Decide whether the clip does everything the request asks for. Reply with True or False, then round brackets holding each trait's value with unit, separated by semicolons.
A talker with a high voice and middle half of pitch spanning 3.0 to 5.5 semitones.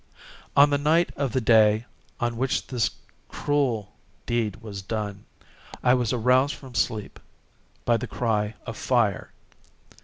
False (120 Hz; 3.4 semitones)